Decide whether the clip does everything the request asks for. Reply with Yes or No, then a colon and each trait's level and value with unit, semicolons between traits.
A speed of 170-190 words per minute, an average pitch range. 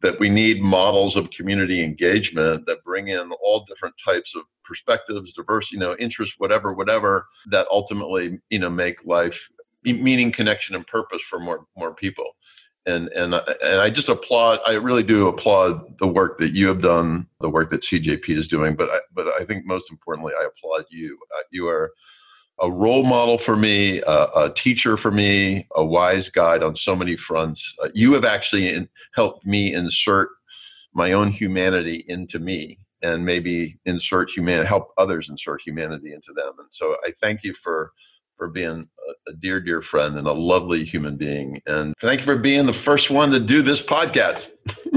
No: average, 185 wpm; wide, 8.5 semitones